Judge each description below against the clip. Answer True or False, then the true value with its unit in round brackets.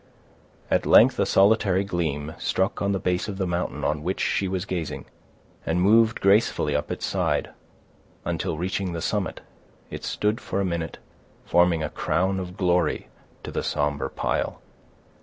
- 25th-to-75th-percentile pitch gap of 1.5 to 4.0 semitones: True (2.9 semitones)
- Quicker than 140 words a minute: True (160 wpm)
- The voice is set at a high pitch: False (90 Hz)